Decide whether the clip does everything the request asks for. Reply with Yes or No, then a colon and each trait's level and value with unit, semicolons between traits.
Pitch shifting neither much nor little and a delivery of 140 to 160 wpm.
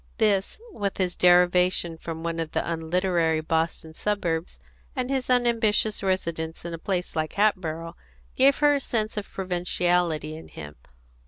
Yes: average, 4.2 semitones; average, 150 wpm